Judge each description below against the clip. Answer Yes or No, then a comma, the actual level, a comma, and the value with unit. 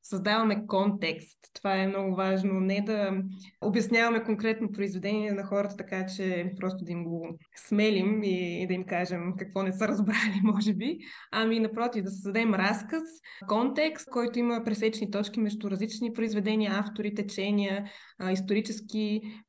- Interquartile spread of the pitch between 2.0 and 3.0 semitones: Yes, narrow, 2.4 semitones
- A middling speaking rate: Yes, average, 140 wpm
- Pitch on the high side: Yes, high, 205 Hz